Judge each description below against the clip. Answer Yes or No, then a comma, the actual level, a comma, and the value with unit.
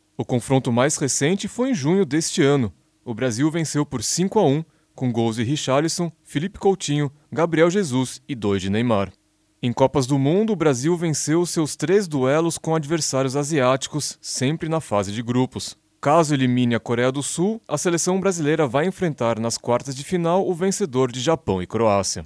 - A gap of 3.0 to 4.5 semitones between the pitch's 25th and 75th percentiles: No, average, 5.1 semitones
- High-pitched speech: No, medium, 145 Hz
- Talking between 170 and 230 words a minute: Yes, average, 180 wpm